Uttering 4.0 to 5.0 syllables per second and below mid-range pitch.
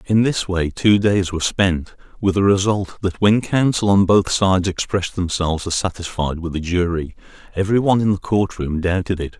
No: 5.4 syllables/s; very low, 95 Hz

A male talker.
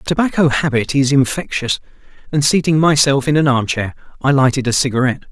Yes: male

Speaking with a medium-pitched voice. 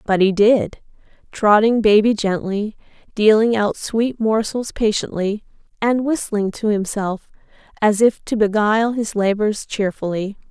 No: high, 215 Hz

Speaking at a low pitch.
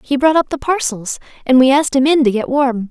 No: very high, 270 Hz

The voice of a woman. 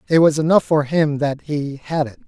No: male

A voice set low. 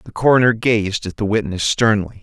Yes: low, 105 Hz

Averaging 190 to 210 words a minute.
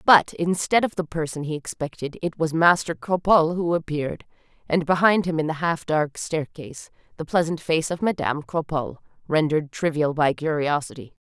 No: average, 165 wpm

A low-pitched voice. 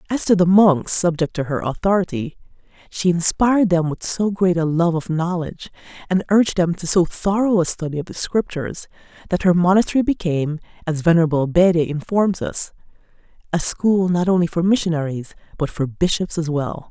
No: medium, 175 Hz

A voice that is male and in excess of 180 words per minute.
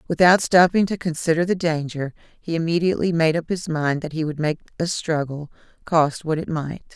No: female; average, 190 wpm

